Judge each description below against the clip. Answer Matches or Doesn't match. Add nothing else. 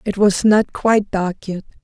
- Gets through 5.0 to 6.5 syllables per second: Doesn't match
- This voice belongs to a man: Doesn't match